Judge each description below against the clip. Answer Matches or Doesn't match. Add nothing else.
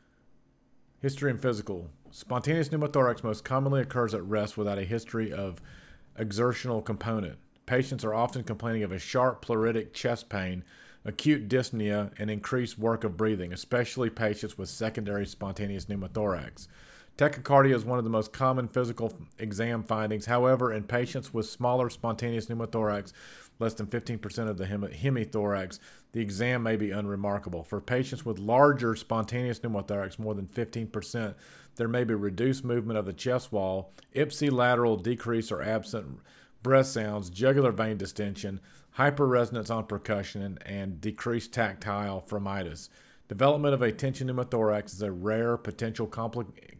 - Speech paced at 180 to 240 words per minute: Doesn't match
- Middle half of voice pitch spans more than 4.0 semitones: Doesn't match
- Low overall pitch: Matches